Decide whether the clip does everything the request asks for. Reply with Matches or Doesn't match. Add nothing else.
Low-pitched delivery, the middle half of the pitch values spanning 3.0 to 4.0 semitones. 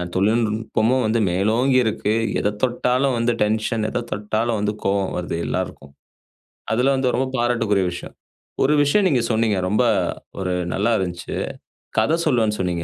Matches